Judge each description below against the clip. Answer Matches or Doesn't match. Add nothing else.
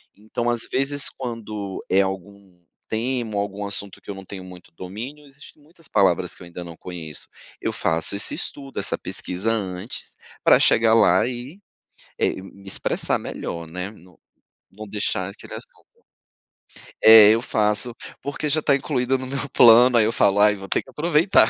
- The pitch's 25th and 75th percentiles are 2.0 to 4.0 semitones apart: Doesn't match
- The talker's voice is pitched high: Doesn't match